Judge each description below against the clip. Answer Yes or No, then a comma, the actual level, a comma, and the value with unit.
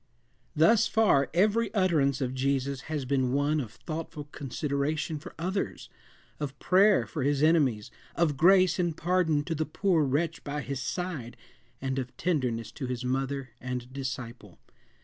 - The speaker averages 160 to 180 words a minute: No, average, 150 wpm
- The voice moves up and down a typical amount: Yes, average, 4.2 semitones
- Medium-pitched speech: Yes, medium, 145 Hz